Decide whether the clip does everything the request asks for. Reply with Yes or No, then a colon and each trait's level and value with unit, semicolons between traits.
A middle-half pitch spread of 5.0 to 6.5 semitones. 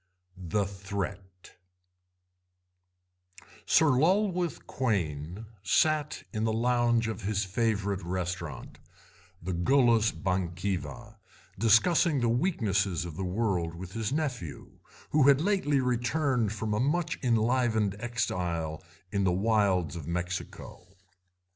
Yes: average, 5.3 semitones